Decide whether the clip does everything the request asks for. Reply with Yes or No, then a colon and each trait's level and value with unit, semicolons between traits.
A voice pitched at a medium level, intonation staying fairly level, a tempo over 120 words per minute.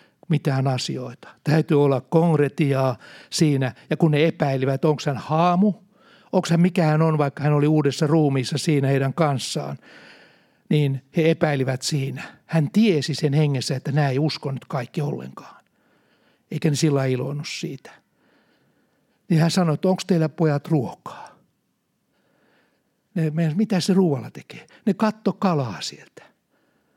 No: medium, 155 Hz; average, 3.1 semitones; average, 135 wpm